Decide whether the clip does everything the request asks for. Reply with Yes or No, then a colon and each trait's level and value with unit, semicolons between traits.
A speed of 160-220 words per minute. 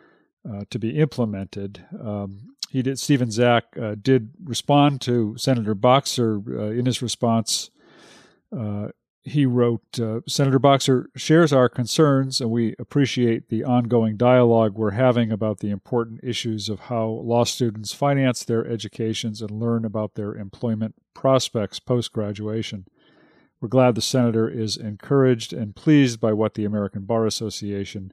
No: average, 145 wpm